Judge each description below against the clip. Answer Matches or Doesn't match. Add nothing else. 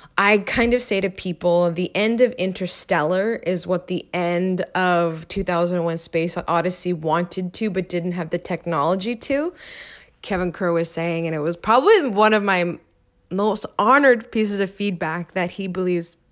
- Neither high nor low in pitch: Matches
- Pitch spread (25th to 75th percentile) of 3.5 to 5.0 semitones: Doesn't match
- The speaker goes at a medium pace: Matches